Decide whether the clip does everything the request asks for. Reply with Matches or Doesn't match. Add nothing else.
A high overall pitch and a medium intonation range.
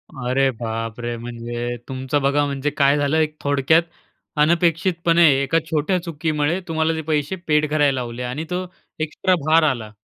Doesn't match